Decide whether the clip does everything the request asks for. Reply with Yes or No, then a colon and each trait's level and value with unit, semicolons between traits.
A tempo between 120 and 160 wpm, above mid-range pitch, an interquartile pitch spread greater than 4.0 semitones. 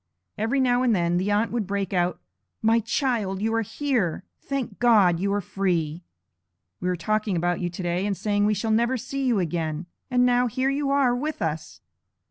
No: average, 195 wpm; high, 210 Hz; wide, 5.5 semitones